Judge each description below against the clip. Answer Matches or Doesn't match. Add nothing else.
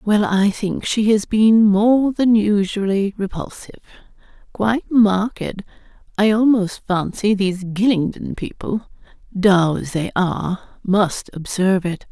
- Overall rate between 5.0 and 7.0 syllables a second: Doesn't match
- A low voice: Doesn't match